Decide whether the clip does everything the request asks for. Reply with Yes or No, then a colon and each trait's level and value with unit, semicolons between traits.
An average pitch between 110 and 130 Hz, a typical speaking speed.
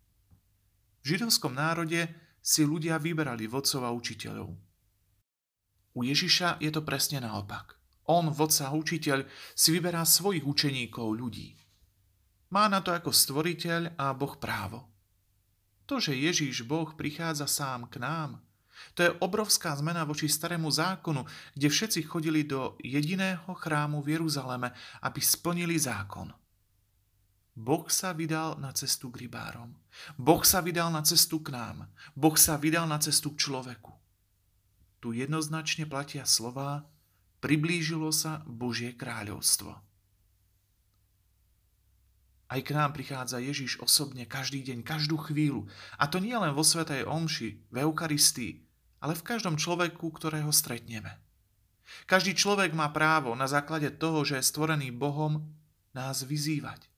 No: medium, 140 Hz; average, 130 wpm